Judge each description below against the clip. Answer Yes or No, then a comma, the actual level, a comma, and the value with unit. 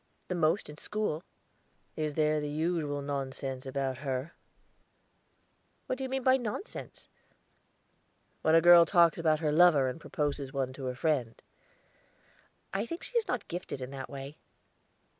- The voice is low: No, medium, 155 Hz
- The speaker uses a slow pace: No, average, 150 wpm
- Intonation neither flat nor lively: Yes, average, 4.2 semitones